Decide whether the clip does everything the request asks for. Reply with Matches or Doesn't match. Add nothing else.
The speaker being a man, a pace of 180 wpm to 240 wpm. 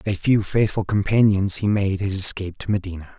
Matches